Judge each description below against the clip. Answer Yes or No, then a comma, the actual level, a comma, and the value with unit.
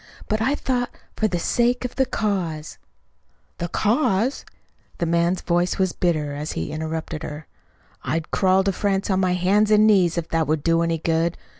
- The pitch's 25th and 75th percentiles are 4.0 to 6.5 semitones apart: Yes, average, 4.3 semitones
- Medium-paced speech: Yes, average, 185 wpm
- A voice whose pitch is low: No, medium, 180 Hz